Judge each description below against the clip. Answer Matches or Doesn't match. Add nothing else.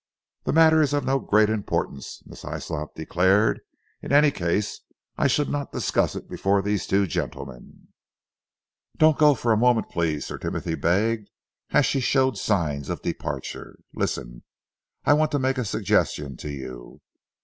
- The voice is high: Doesn't match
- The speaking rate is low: Doesn't match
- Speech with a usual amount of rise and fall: Doesn't match